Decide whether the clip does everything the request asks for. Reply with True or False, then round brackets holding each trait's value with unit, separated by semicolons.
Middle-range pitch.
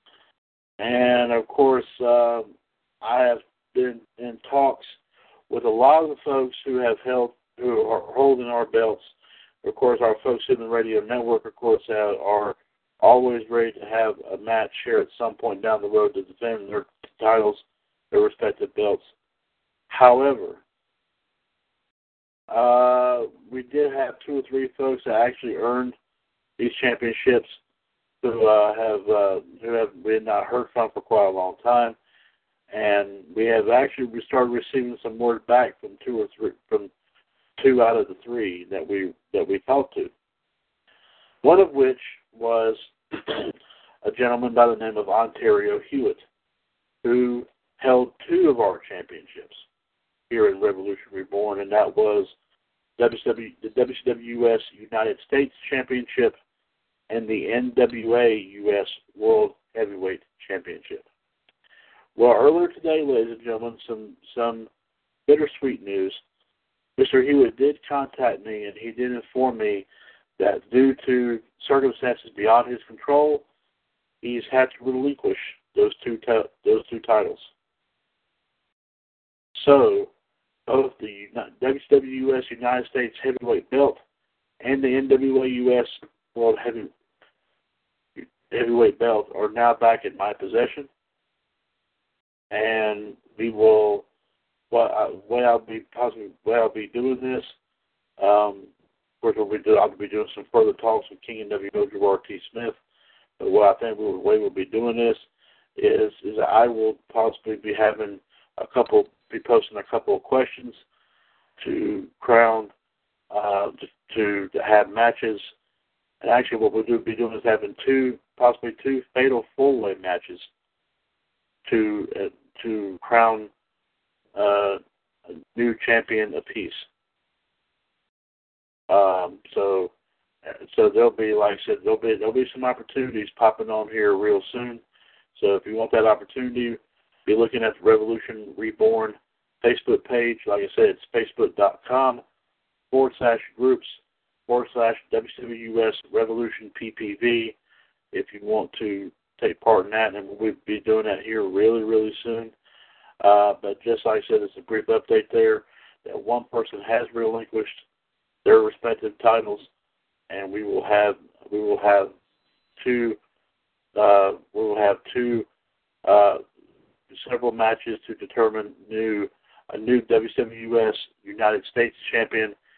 False (125 Hz)